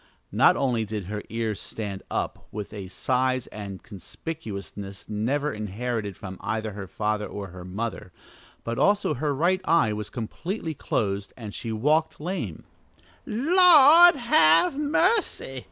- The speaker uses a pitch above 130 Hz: No, low, 115 Hz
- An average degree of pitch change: No, wide, 7.7 semitones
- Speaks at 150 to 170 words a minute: No, average, 140 wpm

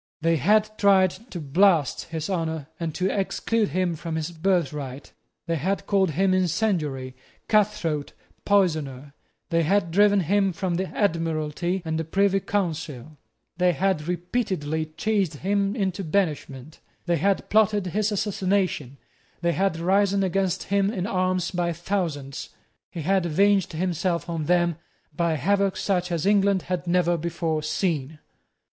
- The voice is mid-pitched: Yes, medium, 180 Hz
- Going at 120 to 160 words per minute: Yes, average, 140 wpm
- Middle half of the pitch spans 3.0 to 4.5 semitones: Yes, average, 3.5 semitones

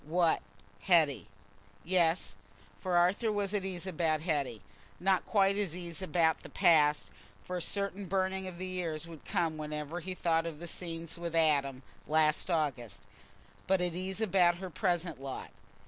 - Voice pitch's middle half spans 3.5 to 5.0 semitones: No, average, 3.1 semitones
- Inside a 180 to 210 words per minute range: No, average, 155 wpm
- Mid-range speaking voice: Yes, medium, 170 Hz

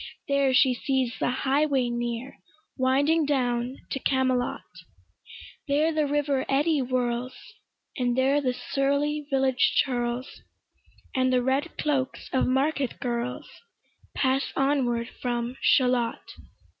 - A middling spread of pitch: No, narrow, 2.1 semitones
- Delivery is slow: Yes, slow, 115 wpm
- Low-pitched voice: No, very high, 260 Hz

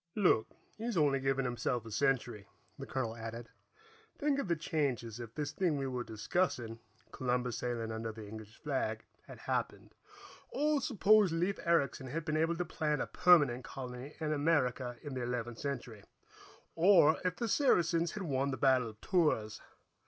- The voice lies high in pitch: No, low, 135 Hz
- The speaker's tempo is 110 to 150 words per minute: No, average, 165 wpm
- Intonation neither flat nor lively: No, wide, 5.7 semitones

